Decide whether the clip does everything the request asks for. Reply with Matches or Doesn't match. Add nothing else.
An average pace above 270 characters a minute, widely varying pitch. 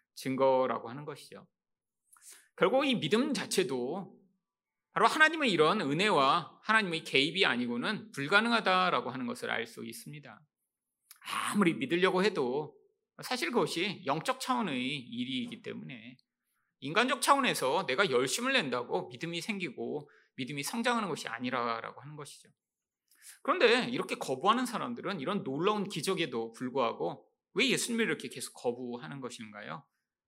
Matches